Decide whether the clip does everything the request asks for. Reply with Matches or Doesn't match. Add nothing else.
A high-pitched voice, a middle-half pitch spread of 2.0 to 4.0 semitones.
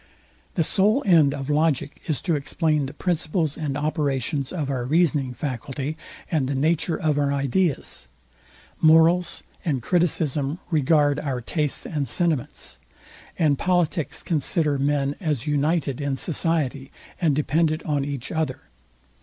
Doesn't match